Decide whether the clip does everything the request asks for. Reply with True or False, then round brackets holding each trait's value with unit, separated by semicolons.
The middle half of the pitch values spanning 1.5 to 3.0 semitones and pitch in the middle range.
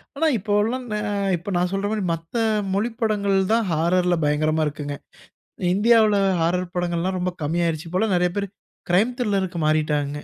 False (4.1 semitones; 180 Hz)